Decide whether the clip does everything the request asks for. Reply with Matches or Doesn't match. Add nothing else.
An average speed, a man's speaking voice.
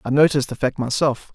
Doesn't match